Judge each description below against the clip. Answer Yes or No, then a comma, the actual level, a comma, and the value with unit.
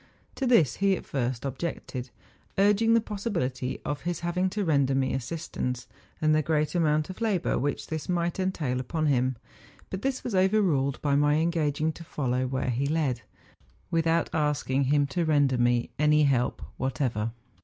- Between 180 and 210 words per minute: No, average, 170 wpm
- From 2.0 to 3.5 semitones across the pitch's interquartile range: No, average, 4.6 semitones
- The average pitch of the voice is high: No, medium, 150 Hz